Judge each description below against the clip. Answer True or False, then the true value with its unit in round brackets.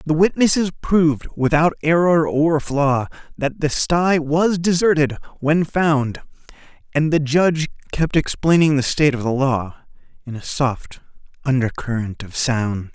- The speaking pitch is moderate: True (145 Hz)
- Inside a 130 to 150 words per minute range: True (145 wpm)